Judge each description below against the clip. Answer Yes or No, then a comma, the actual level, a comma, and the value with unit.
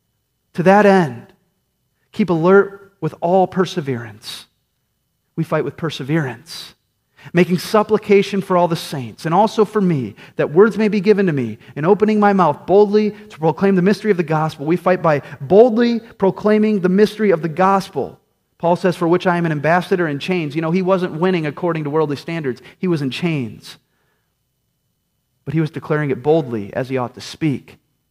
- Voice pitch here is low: No, medium, 175 Hz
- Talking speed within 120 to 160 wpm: No, average, 180 wpm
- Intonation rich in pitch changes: No, average, 5.0 semitones